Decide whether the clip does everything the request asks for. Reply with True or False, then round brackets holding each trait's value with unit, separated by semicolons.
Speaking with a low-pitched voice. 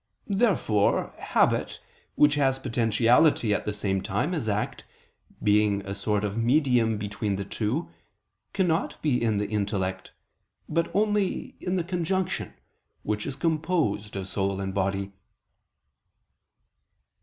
True (110 Hz)